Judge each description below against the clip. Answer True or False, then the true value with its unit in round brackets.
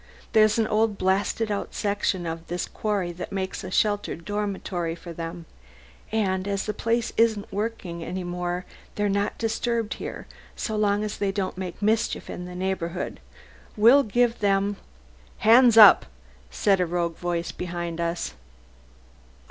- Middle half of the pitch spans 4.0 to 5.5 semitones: False (3.3 semitones)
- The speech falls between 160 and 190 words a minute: False (150 wpm)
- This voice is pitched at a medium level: False (195 Hz)